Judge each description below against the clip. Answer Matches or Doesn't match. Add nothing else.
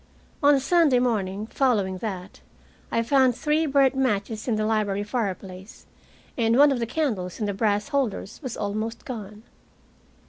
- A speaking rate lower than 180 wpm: Matches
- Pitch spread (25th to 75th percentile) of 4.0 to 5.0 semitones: Matches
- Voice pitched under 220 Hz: Doesn't match